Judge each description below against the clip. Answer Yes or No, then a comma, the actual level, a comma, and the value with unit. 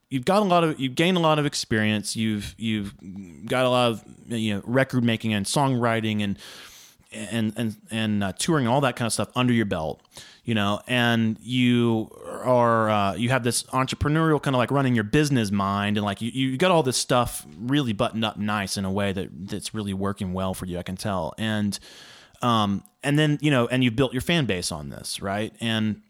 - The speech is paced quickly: Yes, fast, 220 wpm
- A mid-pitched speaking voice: No, low, 115 Hz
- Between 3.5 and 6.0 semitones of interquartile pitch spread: Yes, average, 3.8 semitones